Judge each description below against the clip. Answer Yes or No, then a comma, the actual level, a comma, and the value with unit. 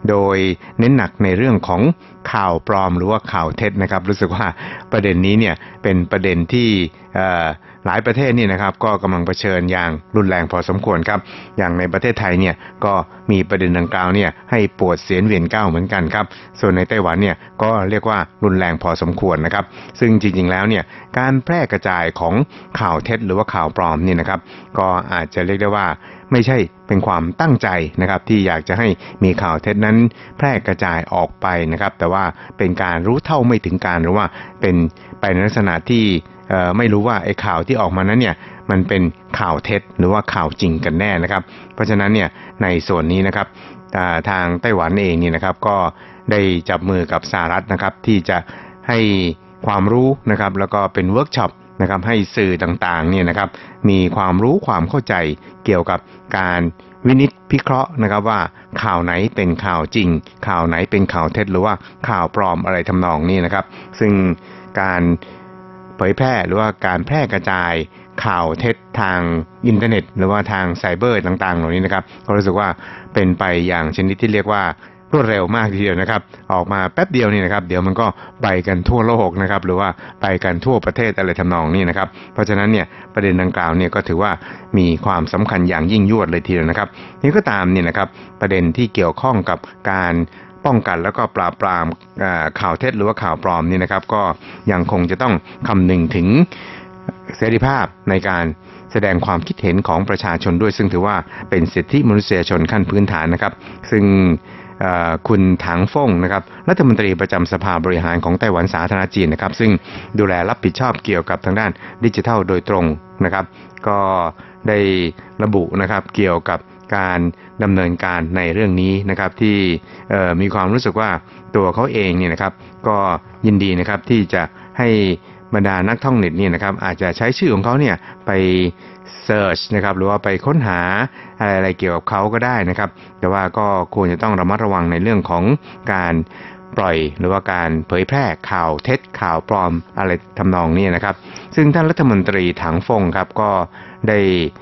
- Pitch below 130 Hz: Yes, very low, 95 Hz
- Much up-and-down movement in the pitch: No, average, 2.9 semitones